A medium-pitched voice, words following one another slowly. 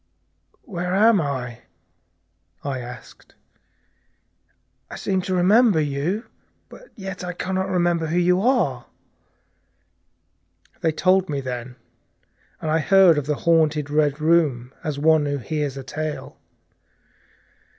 Yes: medium, 160 Hz; slow, 125 wpm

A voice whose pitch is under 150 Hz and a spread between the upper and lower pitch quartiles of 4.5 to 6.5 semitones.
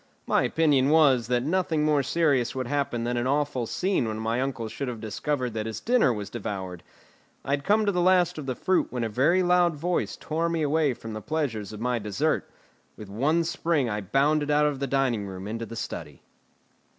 Yes: low, 135 Hz; wide, 5.5 semitones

